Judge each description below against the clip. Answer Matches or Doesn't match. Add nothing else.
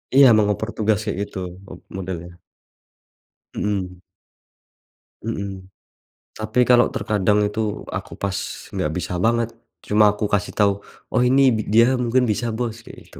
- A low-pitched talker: Matches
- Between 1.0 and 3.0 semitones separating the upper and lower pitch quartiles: Matches